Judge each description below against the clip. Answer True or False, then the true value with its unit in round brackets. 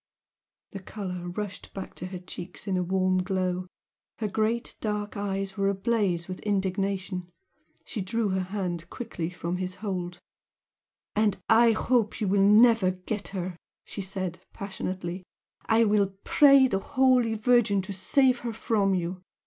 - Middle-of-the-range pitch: False (195 Hz)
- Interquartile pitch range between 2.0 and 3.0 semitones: True (2.7 semitones)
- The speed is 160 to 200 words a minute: False (150 wpm)